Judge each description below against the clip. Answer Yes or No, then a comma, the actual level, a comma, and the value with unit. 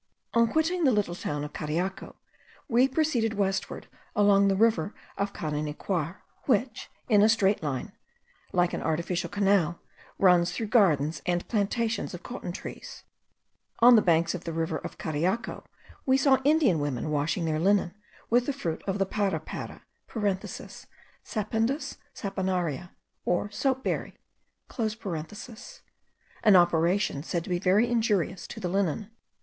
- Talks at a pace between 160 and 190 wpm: No, average, 140 wpm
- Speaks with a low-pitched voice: No, high, 195 Hz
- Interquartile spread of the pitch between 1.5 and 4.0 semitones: No, average, 4.9 semitones